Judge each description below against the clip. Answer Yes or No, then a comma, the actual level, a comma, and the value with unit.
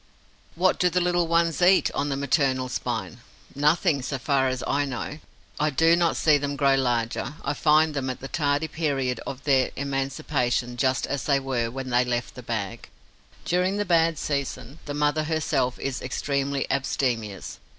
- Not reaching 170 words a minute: No, average, 175 wpm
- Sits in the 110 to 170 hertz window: Yes, medium, 140 Hz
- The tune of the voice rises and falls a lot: No, average, 3.2 semitones